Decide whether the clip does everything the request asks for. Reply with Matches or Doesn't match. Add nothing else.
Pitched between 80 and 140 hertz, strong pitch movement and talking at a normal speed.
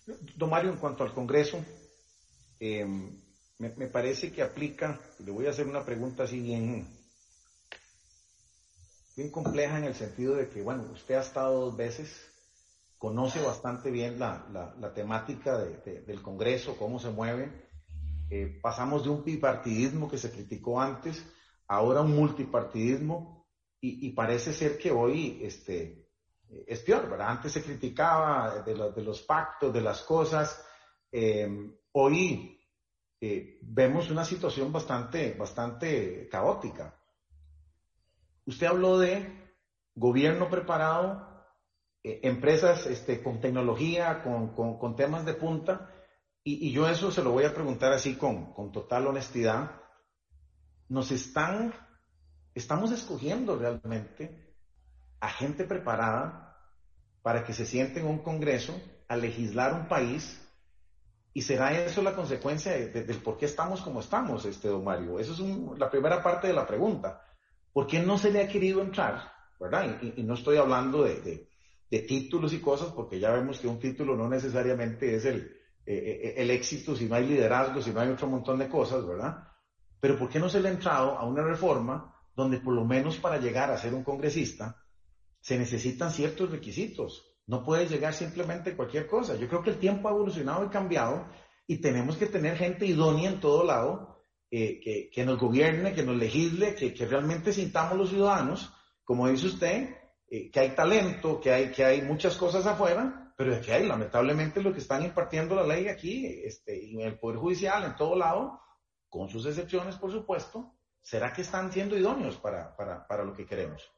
Matches